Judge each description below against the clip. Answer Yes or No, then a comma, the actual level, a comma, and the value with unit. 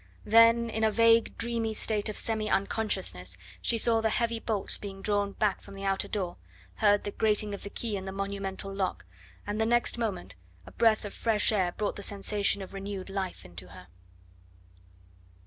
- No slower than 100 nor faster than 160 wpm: No, average, 185 wpm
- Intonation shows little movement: Yes, narrow, 2.2 semitones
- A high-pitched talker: Yes, high, 205 Hz